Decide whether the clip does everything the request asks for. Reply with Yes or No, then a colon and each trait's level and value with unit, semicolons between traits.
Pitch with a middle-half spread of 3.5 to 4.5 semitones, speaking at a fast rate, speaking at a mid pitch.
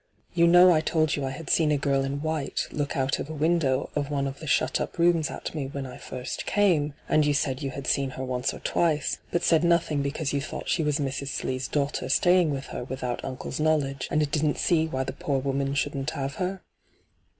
No: narrow, 2.5 semitones; fast, 230 wpm; medium, 145 Hz